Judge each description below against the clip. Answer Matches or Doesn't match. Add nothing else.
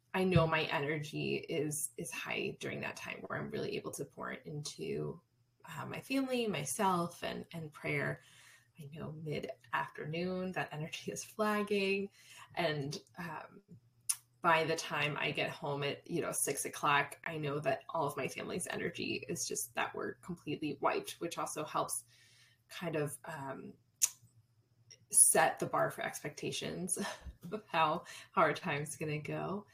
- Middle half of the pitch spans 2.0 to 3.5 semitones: Doesn't match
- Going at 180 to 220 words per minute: Doesn't match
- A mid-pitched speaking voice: Matches